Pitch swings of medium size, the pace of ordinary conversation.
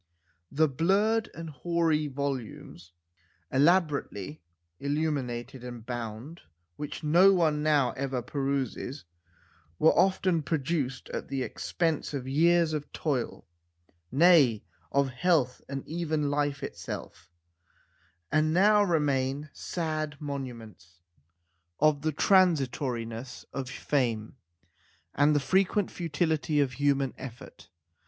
No: average, 3.7 semitones; slow, 105 wpm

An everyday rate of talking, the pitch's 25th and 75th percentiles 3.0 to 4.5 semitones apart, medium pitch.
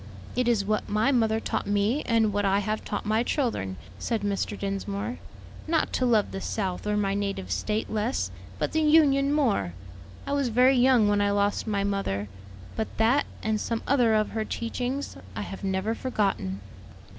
No: average, 180 wpm; average, 3.4 semitones; high, 215 Hz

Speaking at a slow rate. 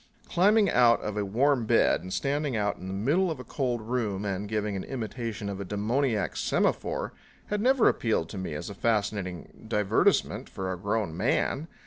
No: average, 185 wpm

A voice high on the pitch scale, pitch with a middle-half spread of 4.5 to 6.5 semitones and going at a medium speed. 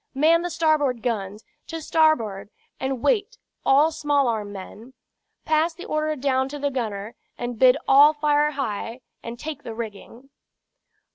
Yes: very high, 275 Hz; average, 4.9 semitones; average, 150 wpm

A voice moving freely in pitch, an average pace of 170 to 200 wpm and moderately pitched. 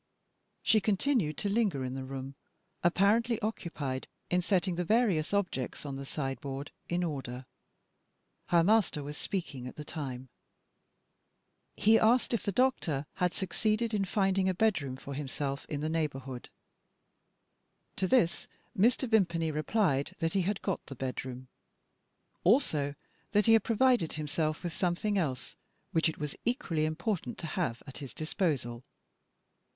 No: wide, 6.5 semitones; average, 150 wpm; medium, 165 Hz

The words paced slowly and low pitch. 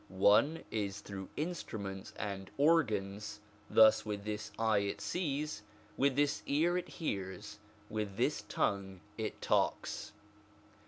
Yes: slow, 125 wpm; low, 105 Hz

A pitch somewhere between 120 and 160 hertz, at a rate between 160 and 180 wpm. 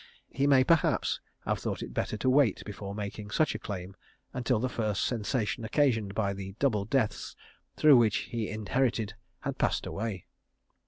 No: low, 110 Hz; average, 165 wpm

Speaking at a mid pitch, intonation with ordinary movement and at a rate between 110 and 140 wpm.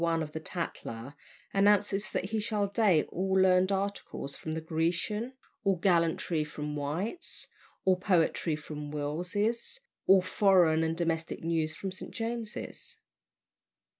Yes: medium, 180 Hz; average, 3.9 semitones; slow, 135 wpm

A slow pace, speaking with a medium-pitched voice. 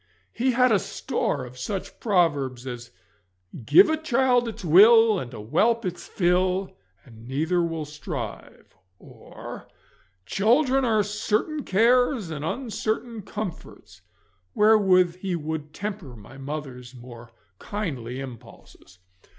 Yes: slow, 120 wpm; medium, 180 Hz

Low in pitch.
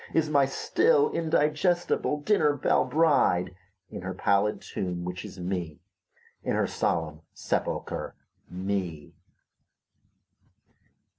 Yes: low, 100 Hz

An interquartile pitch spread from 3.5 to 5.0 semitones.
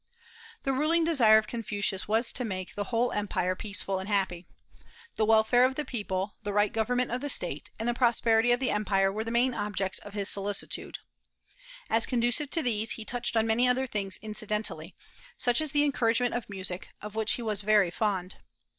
No: average, 3.1 semitones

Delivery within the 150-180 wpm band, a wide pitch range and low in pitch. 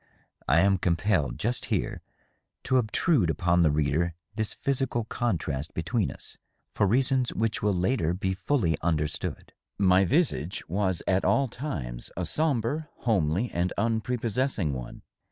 No: slow, 135 wpm; wide, 6.5 semitones; very low, 95 Hz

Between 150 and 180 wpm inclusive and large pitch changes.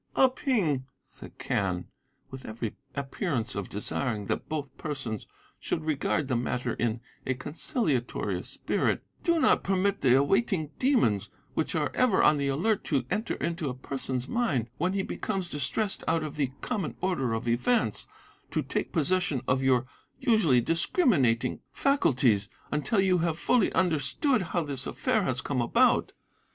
Yes: average, 155 wpm; wide, 7.1 semitones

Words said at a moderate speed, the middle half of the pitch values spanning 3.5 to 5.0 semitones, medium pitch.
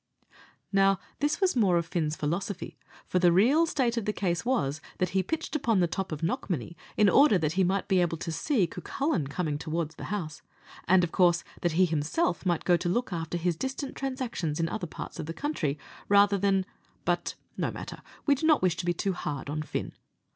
No: fast, 210 wpm; average, 4.7 semitones; medium, 180 Hz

